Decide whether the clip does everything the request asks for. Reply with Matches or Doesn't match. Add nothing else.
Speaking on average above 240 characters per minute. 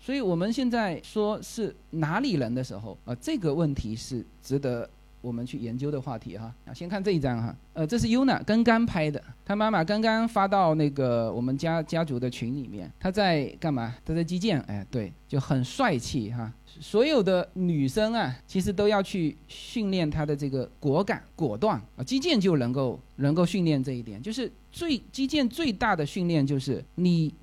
Matches